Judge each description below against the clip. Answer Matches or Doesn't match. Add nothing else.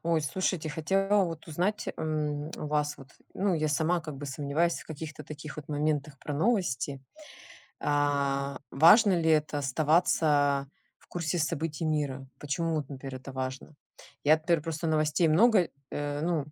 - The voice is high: Doesn't match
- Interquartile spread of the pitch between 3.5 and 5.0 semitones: Doesn't match